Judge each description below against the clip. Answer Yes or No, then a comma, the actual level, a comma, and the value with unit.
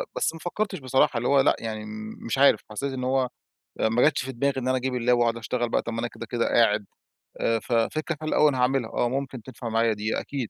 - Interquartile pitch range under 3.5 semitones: Yes, average, 2.8 semitones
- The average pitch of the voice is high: No, low, 125 Hz